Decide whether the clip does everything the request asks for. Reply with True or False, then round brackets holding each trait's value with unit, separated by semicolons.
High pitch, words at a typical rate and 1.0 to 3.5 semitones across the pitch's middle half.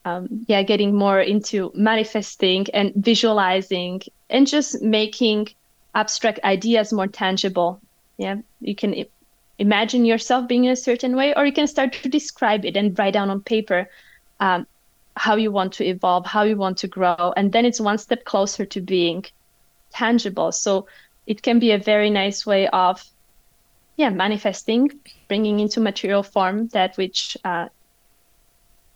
True (205 Hz; 155 wpm; 2.9 semitones)